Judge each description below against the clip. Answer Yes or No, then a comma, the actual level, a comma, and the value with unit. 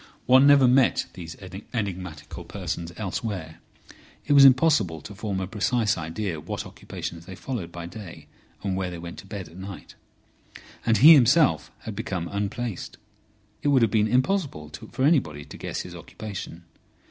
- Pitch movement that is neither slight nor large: No, wide, 6.2 semitones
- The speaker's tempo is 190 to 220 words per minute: No, average, 160 wpm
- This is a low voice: Yes, low, 100 Hz